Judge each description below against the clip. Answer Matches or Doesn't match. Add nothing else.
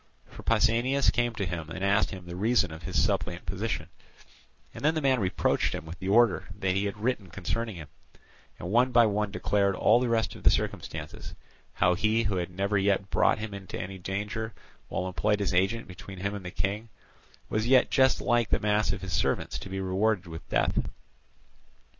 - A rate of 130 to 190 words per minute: Doesn't match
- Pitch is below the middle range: Matches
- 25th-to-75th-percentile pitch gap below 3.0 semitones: Doesn't match